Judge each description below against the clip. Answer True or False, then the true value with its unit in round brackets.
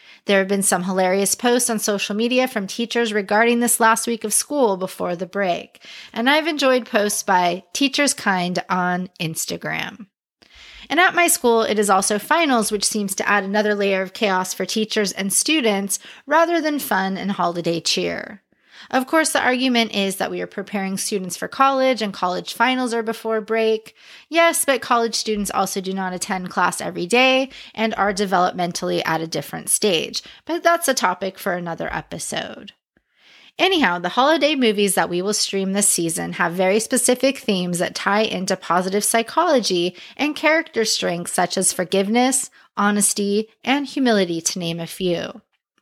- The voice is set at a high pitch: True (210 Hz)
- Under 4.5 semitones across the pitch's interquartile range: False (4.9 semitones)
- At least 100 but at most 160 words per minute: False (170 wpm)